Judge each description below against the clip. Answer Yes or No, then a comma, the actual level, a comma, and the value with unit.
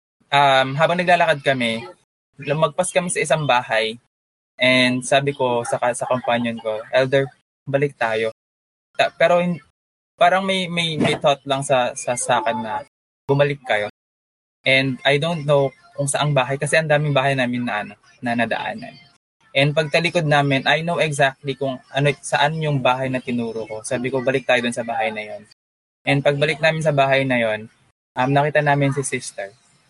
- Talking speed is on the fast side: Yes, fast, 175 wpm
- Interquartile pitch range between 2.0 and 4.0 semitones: Yes, average, 3.6 semitones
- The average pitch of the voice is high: No, low, 135 Hz